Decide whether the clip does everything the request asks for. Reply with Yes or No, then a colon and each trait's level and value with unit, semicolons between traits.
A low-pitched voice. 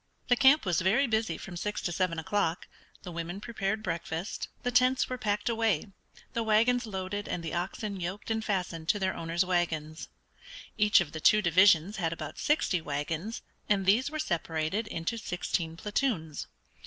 No: high, 190 Hz